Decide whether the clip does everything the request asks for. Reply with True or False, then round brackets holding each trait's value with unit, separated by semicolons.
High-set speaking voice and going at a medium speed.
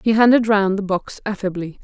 True (205 Hz; 195 wpm)